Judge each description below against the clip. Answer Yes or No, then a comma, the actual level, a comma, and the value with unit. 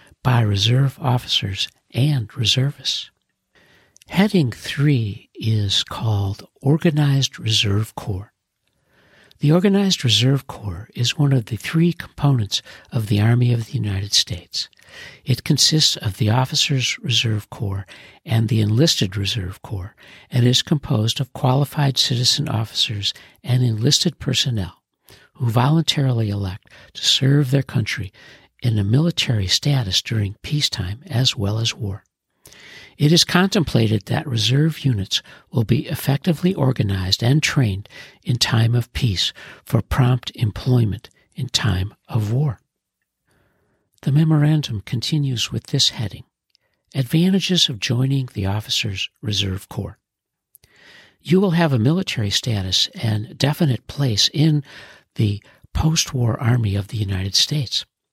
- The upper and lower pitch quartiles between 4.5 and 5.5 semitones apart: Yes, average, 5.1 semitones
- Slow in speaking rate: Yes, slow, 125 wpm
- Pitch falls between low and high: No, low, 125 Hz